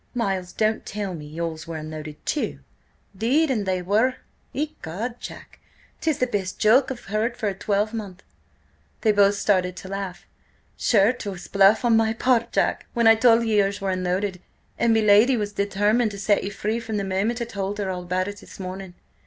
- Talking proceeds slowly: No, average, 195 wpm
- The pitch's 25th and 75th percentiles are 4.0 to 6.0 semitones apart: No, average, 3.2 semitones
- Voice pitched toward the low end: No, high, 205 Hz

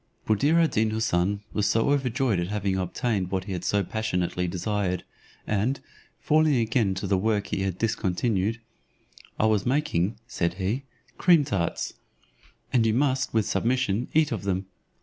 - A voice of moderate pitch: No, low, 105 Hz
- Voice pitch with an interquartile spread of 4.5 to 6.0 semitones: Yes, average, 4.8 semitones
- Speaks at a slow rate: No, average, 155 wpm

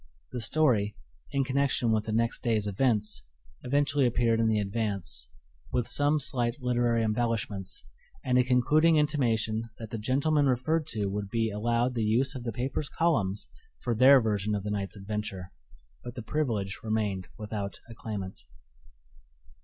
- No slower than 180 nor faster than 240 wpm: No, average, 155 wpm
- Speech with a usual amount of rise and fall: Yes, average, 3.5 semitones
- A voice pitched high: No, low, 115 Hz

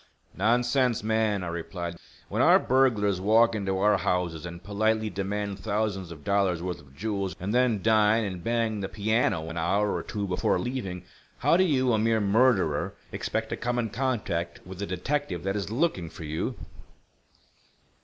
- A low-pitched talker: Yes, low, 105 Hz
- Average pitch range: Yes, average, 3.7 semitones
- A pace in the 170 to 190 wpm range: Yes, average, 175 wpm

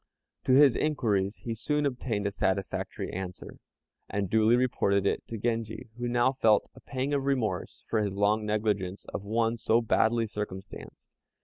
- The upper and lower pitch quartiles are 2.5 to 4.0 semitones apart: Yes, average, 3.1 semitones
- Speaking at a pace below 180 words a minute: Yes, average, 165 wpm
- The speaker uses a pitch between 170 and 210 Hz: No, low, 110 Hz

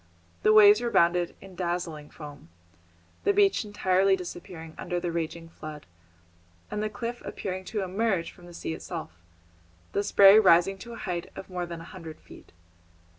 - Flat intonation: No, average, 3.2 semitones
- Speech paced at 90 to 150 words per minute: No, average, 165 wpm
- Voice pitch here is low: No, medium, 180 Hz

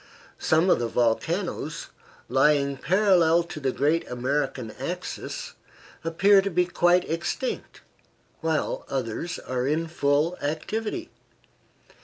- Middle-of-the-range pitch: Yes, medium, 160 Hz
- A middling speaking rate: No, slow, 110 wpm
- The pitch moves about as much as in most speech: Yes, average, 4.3 semitones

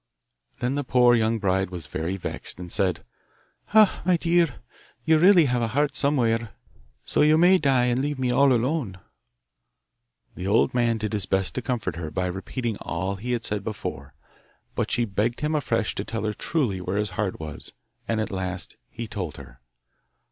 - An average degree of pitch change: No, wide, 5.7 semitones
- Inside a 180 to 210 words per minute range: Yes, average, 185 wpm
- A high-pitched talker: No, low, 115 Hz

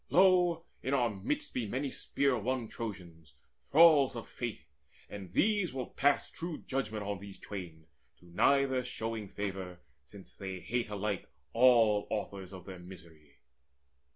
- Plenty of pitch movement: Yes, wide, 5.8 semitones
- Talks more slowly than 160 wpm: Yes, average, 145 wpm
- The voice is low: Yes, low, 105 Hz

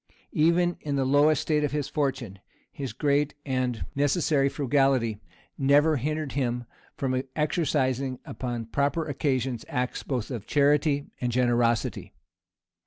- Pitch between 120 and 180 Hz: Yes, low, 135 Hz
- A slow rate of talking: Yes, slow, 125 wpm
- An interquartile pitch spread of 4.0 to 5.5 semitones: No, average, 2.7 semitones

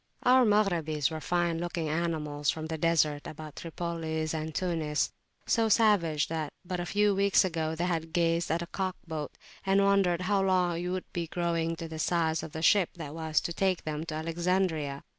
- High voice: No, medium, 165 Hz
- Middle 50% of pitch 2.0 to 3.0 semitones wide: Yes, narrow, 2.5 semitones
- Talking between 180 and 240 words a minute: Yes, average, 195 wpm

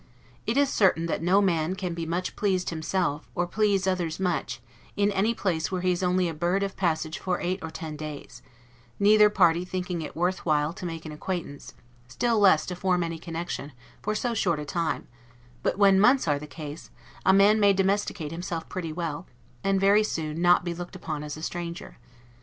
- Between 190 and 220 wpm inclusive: Yes, average, 200 wpm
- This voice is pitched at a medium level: Yes, medium, 175 Hz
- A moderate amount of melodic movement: Yes, average, 3.0 semitones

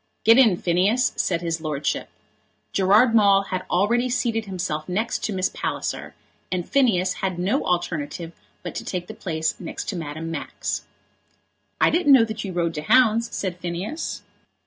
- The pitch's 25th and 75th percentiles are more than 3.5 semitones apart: Yes, average, 4.6 semitones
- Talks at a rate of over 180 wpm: No, average, 165 wpm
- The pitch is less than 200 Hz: Yes, medium, 185 Hz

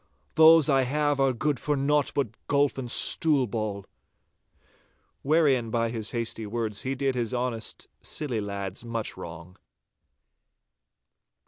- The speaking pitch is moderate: No, low, 125 Hz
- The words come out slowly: Yes, slow, 130 wpm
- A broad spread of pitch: No, average, 4.3 semitones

